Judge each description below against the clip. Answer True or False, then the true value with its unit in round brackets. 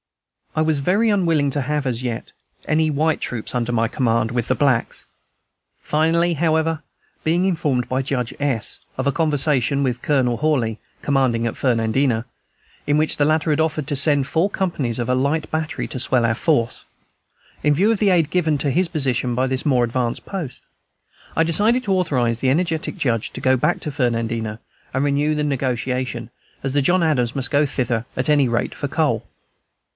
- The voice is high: False (140 Hz)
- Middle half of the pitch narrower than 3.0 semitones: False (4.2 semitones)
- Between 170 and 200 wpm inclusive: True (185 wpm)